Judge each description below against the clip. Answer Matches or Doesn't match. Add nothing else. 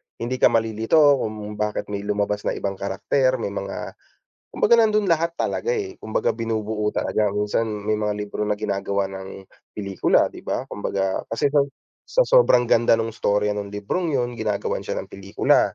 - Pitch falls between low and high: Doesn't match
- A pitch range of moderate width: Matches